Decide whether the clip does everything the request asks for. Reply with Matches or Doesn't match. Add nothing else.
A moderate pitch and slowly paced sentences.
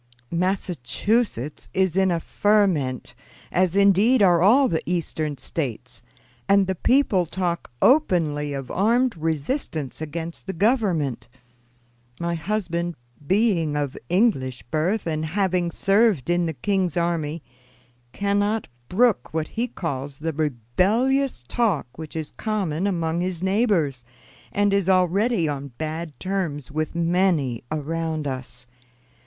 Matches